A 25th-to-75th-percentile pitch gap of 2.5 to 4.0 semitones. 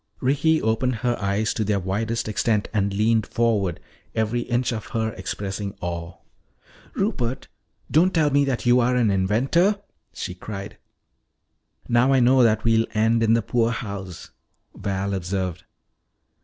Yes: average, 3.6 semitones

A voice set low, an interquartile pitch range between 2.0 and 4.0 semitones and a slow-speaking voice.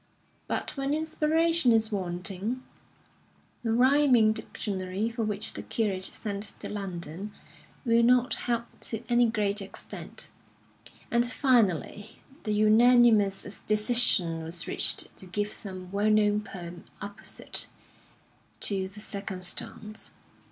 No: high, 215 Hz; average, 3.4 semitones; slow, 115 wpm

